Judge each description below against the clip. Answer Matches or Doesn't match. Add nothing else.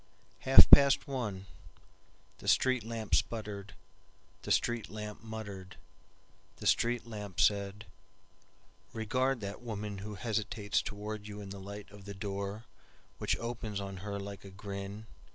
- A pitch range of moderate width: Doesn't match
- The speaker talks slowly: Matches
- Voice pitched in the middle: Doesn't match